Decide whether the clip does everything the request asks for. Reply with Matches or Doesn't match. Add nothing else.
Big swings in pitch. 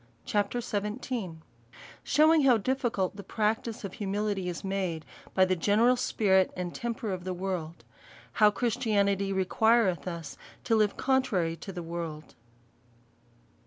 Doesn't match